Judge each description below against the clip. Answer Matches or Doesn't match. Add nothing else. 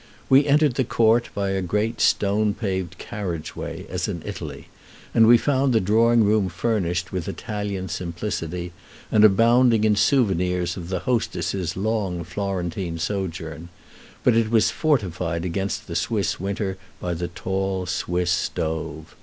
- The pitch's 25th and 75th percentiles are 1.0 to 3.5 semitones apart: Doesn't match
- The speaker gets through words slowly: Doesn't match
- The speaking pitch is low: Matches